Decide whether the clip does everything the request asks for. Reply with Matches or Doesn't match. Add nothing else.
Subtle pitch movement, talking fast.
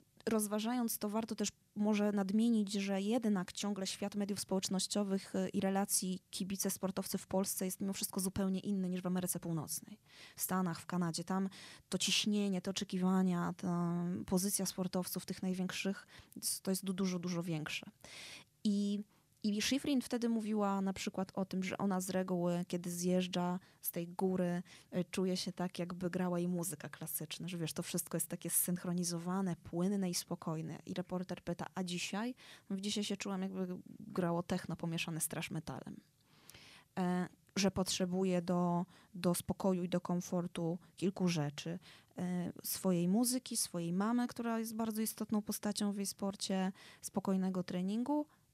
Doesn't match